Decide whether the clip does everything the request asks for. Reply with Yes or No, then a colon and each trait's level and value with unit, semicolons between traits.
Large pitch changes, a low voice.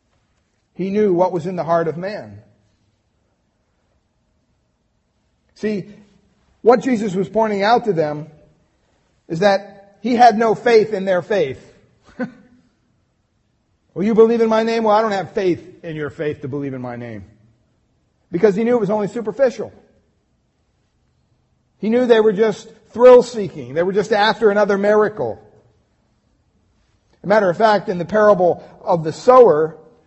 No: wide, 6.6 semitones; high, 200 Hz